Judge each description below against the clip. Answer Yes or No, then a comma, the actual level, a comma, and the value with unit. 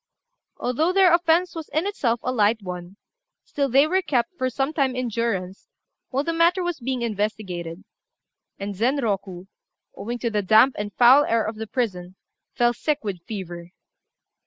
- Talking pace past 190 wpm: No, average, 165 wpm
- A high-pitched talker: Yes, high, 235 Hz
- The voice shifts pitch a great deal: Yes, wide, 5.9 semitones